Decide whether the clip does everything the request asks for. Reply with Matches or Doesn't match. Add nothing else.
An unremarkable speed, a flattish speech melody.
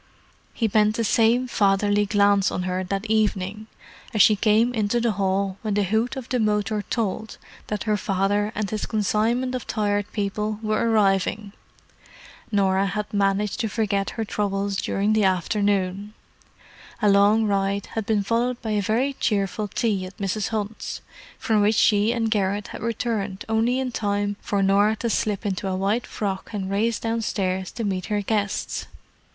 Matches